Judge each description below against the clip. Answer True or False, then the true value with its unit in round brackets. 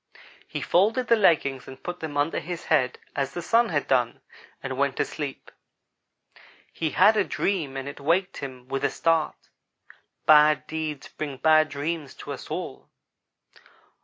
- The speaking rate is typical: True (160 wpm)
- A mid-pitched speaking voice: True (155 Hz)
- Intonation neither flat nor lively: True (3.7 semitones)